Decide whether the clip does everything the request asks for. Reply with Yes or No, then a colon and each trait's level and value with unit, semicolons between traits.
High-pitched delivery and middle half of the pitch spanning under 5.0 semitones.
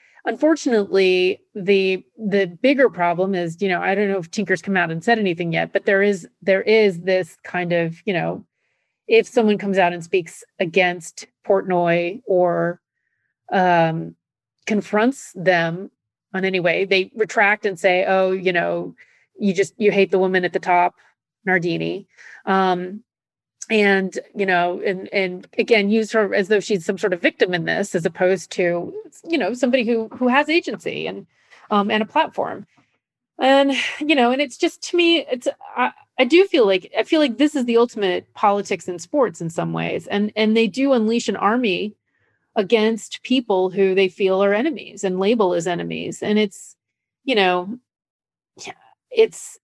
Yes: high, 200 Hz; average, 4.2 semitones